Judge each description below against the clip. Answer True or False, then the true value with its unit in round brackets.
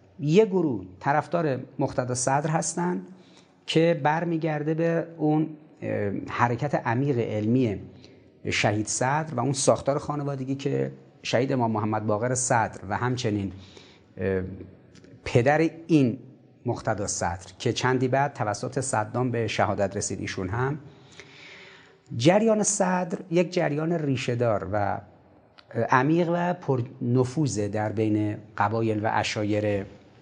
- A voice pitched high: False (130 Hz)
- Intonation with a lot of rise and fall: True (6.2 semitones)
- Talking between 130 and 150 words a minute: False (110 wpm)